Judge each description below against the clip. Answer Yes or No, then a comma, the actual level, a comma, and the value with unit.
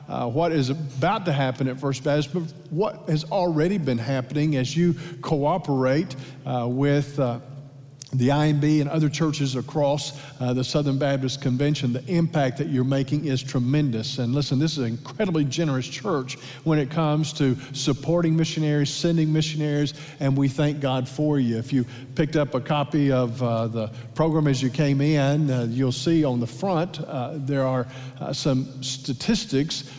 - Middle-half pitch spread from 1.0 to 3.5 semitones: Yes, average, 2.7 semitones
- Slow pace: No, average, 175 wpm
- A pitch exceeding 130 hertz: Yes, medium, 140 Hz